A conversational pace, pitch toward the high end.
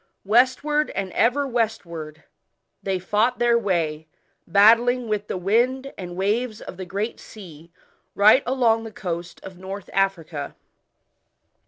No: slow, 130 wpm; high, 205 Hz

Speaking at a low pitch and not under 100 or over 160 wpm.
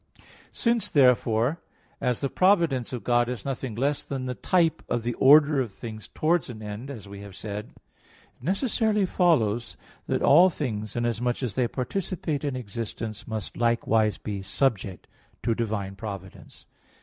Yes: low, 120 Hz; average, 155 wpm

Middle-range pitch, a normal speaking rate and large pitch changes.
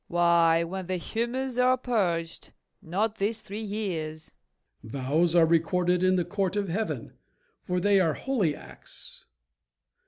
No: medium, 180 Hz; average, 150 wpm; average, 4.0 semitones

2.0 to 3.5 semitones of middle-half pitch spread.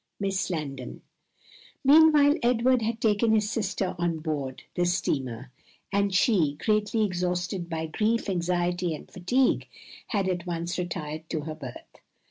No: average, 4.9 semitones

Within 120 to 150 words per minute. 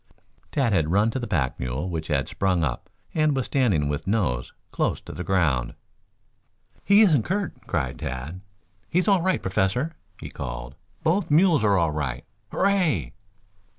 No: average, 165 wpm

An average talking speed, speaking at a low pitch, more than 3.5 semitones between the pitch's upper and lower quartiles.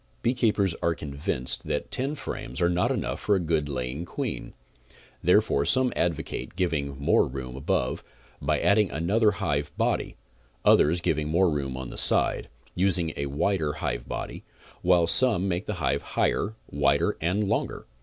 Yes: average, 155 wpm; very low, 85 Hz; average, 5.2 semitones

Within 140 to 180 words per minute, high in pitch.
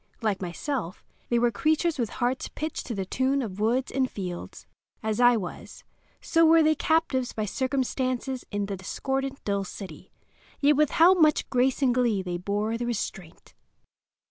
Yes: average, 165 wpm; high, 245 Hz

